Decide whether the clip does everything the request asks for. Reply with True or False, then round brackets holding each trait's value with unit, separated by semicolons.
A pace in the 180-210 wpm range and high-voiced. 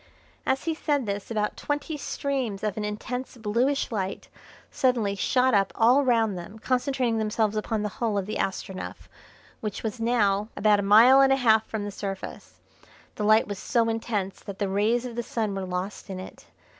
True (190 wpm; 220 Hz)